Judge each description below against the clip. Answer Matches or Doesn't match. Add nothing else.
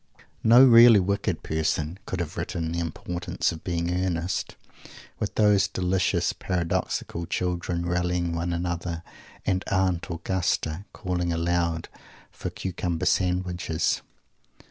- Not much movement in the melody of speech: Matches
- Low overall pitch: Matches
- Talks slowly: Matches